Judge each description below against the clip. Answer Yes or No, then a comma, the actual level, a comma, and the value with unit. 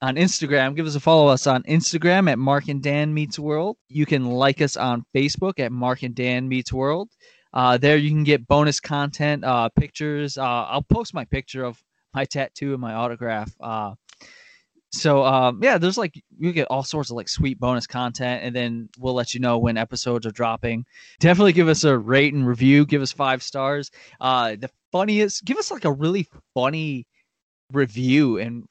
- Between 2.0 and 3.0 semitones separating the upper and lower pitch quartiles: No, average, 3.4 semitones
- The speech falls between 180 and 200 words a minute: Yes, average, 195 wpm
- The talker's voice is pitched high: No, low, 135 Hz